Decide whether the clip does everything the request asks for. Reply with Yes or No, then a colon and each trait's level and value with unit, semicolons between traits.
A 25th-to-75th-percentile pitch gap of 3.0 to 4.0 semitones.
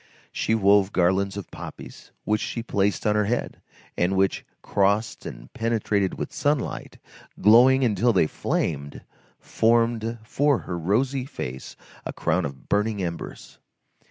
Yes: average, 3.5 semitones